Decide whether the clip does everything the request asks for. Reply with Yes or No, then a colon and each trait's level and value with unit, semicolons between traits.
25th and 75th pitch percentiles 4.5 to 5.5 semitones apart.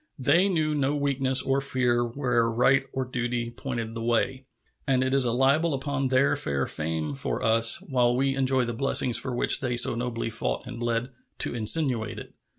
No: narrow, 2.5 semitones